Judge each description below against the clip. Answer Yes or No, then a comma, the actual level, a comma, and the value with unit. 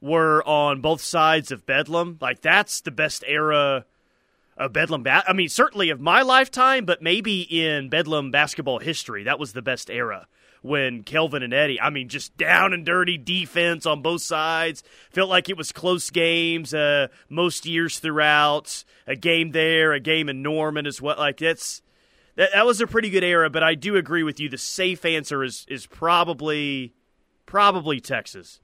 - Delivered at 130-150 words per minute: No, average, 180 wpm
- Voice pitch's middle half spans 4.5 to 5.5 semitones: No, average, 2.7 semitones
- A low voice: No, medium, 160 Hz